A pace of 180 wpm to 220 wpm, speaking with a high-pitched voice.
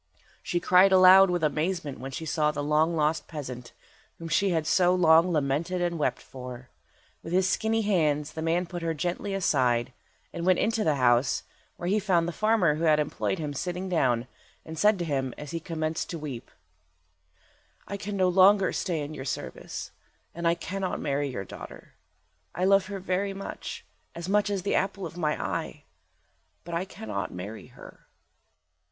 No: average, 185 wpm; medium, 170 Hz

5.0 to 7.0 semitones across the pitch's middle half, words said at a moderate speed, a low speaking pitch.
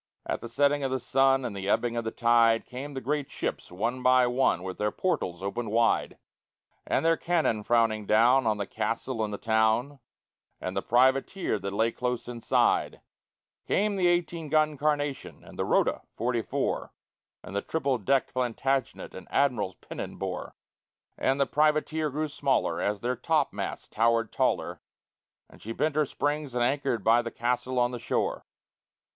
No: average, 3.9 semitones; average, 175 wpm; low, 125 Hz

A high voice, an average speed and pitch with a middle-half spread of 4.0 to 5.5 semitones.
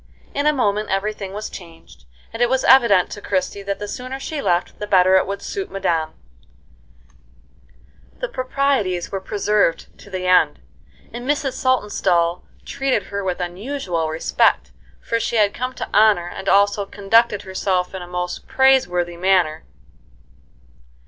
Yes: high, 200 Hz; average, 155 wpm; average, 5.1 semitones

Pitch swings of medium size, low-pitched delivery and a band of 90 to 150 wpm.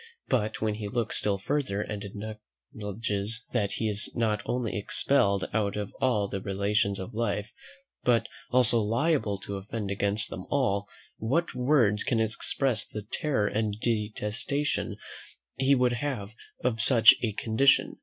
Yes: average, 3.2 semitones; low, 110 Hz; average, 145 wpm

